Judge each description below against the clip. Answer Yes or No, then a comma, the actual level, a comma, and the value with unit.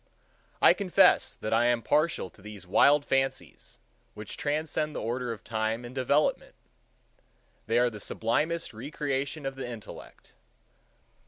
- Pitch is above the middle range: No, low, 125 Hz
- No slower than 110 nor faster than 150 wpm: Yes, average, 140 wpm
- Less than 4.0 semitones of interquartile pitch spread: No, average, 4.7 semitones